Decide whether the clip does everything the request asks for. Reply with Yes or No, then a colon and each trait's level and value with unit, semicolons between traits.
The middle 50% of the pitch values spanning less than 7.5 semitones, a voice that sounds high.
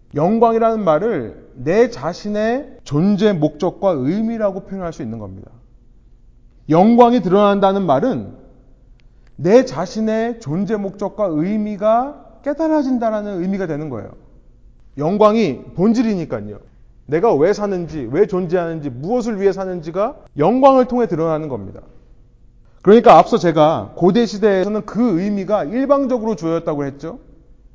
Yes: wide, 6.3 semitones; high, 195 Hz